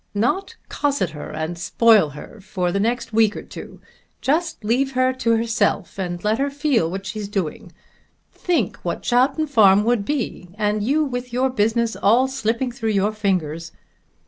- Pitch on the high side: Yes, high, 225 Hz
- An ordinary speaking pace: Yes, average, 170 wpm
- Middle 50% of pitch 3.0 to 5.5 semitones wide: Yes, average, 4.7 semitones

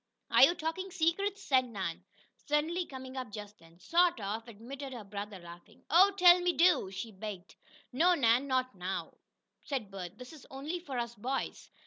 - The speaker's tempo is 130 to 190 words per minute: Yes, average, 175 wpm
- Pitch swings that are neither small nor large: No, wide, 8.1 semitones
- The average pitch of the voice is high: Yes, very high, 255 Hz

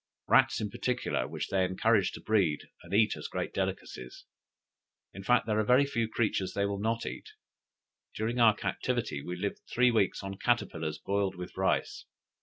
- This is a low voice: Yes, low, 100 Hz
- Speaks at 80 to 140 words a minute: No, average, 175 wpm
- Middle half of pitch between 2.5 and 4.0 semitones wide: Yes, average, 3.4 semitones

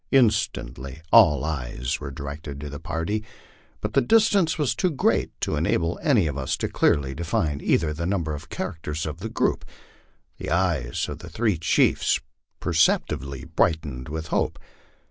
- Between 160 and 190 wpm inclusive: Yes, average, 165 wpm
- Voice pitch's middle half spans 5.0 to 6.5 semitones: Yes, wide, 5.4 semitones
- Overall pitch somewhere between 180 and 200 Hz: No, very low, 80 Hz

